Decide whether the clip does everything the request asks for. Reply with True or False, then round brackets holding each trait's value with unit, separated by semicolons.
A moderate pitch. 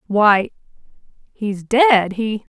False (215 Hz)